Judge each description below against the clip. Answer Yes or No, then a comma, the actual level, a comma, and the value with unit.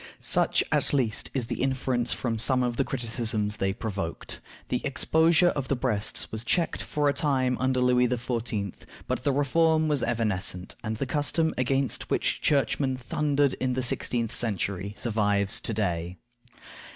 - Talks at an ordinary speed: Yes, average, 160 wpm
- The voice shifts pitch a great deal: No, average, 4.0 semitones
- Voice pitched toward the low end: Yes, low, 125 Hz